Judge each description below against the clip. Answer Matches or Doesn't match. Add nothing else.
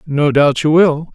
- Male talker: Matches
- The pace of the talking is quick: Matches